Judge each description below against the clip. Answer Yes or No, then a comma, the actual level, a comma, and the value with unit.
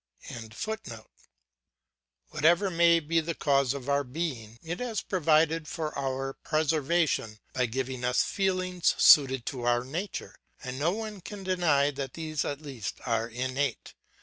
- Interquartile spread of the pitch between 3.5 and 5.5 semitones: Yes, average, 4.7 semitones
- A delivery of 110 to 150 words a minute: Yes, average, 145 wpm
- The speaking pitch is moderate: Yes, medium, 145 Hz